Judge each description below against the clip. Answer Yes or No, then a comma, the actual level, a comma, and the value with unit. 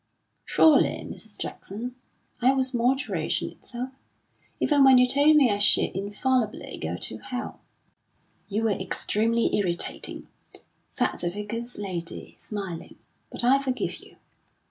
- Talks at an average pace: No, slow, 125 wpm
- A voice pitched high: Yes, high, 235 Hz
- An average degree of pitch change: Yes, average, 4.3 semitones